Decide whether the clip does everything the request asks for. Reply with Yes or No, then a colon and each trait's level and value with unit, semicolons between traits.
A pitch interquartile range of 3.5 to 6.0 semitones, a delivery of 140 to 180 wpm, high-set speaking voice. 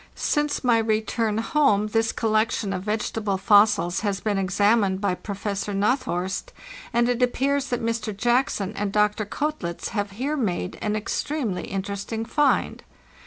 No: average, 3.1 semitones; average, 145 wpm; high, 215 Hz